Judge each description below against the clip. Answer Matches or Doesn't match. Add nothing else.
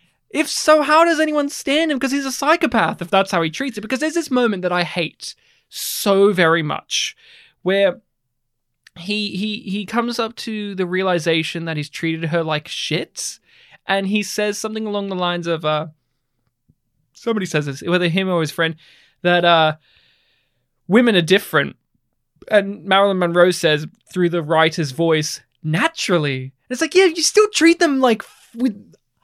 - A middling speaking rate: Matches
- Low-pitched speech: Doesn't match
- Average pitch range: Doesn't match